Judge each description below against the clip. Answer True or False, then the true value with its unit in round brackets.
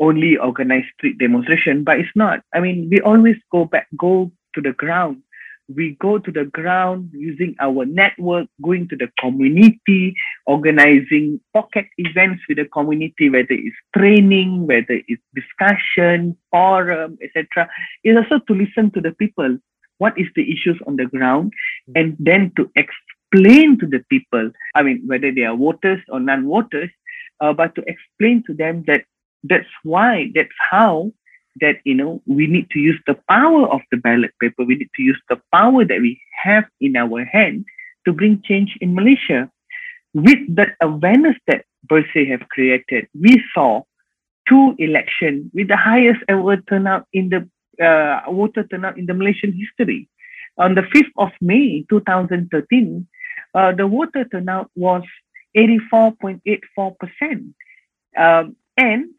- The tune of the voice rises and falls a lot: True (5.8 semitones)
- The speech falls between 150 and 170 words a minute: True (160 wpm)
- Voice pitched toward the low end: False (185 Hz)